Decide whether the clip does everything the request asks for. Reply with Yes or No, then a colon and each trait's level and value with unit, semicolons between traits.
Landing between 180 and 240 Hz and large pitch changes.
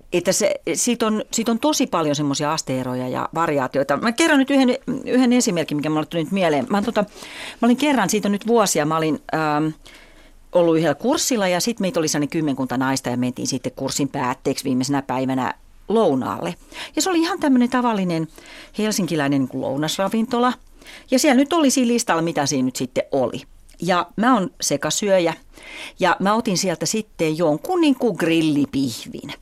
Yes: medium, 185 Hz; wide, 8.9 semitones